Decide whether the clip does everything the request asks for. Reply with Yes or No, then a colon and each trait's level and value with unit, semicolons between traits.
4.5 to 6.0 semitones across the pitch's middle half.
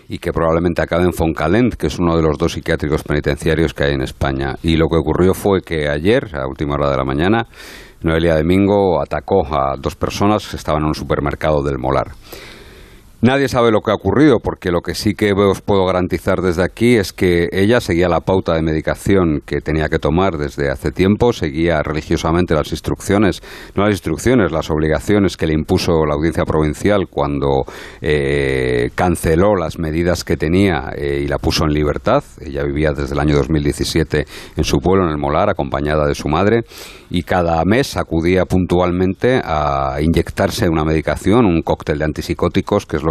No: average, 3.8 semitones